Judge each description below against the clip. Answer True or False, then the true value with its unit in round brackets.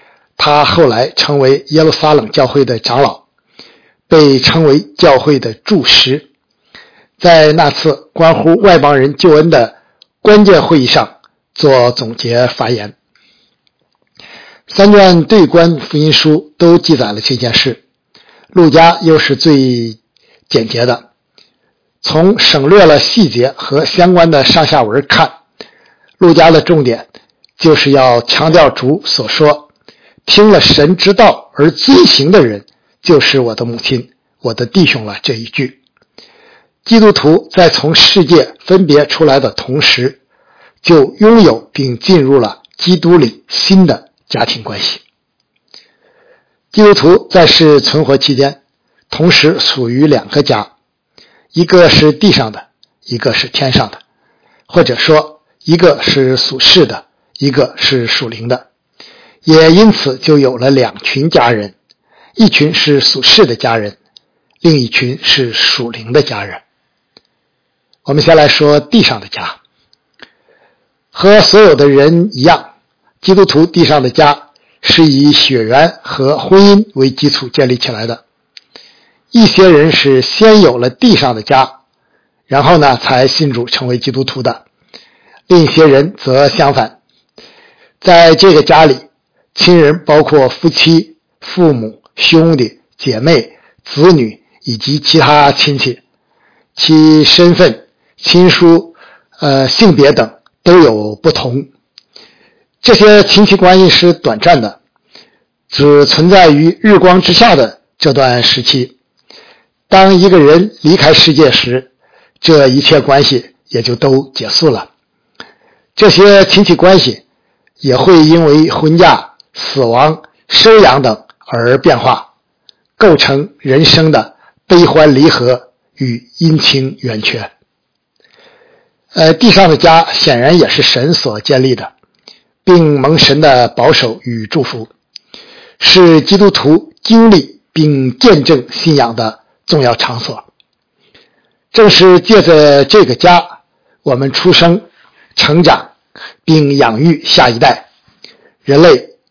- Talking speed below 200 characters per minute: True (185 characters per minute)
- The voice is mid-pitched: True (155 Hz)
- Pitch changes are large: False (4.8 semitones)